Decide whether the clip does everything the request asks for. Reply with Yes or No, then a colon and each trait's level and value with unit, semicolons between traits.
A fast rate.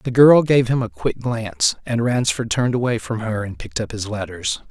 Yes: fast, 230 wpm